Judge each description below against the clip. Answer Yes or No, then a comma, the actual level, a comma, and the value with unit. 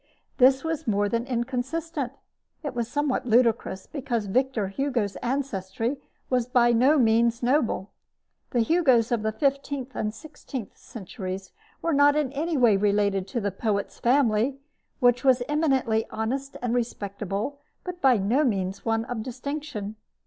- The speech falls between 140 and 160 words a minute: Yes, average, 145 wpm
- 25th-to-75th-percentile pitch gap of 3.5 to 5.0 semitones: Yes, average, 4.1 semitones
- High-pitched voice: Yes, high, 245 Hz